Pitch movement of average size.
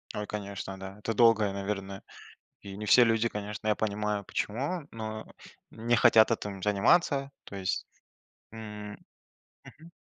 No: narrow, 2.1 semitones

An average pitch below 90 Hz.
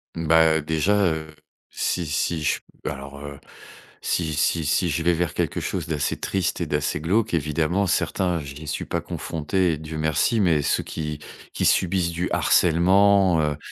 Yes: very low, 80 Hz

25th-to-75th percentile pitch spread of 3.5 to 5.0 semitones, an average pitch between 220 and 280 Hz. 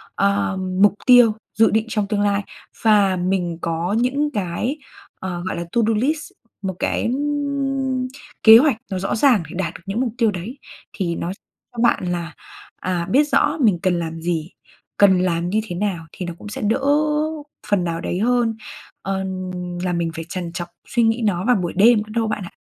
No: average, 4.3 semitones; high, 195 Hz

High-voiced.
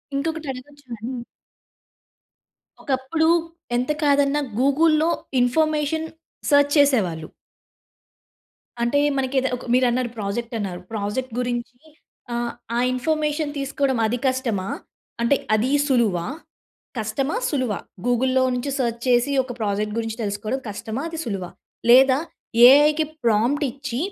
Yes: very high, 255 Hz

